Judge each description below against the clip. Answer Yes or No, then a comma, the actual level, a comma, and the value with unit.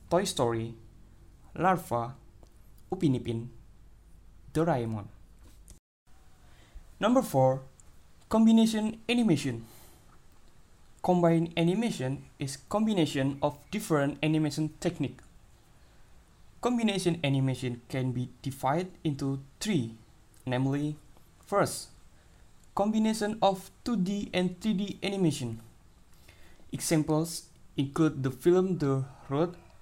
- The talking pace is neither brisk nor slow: No, slow, 85 wpm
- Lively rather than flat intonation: Yes, wide, 7.5 semitones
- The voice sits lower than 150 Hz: Yes, medium, 140 Hz